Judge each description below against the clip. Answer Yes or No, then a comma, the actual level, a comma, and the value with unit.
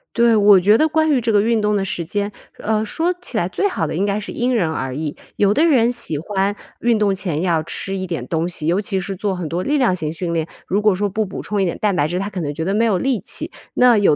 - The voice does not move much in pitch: No, average, 4.1 semitones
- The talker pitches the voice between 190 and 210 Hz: Yes, high, 200 Hz